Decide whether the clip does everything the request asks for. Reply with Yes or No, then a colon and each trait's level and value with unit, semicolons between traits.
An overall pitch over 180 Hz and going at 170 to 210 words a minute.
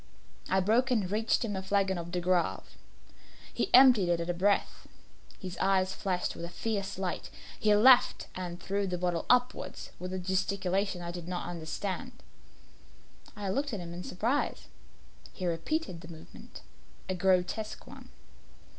No: high, 190 Hz; average, 160 wpm